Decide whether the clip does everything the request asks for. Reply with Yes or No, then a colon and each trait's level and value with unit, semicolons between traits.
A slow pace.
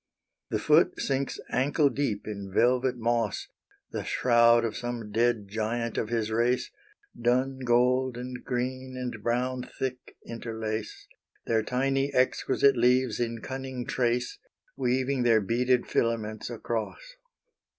Yes: slow, 125 wpm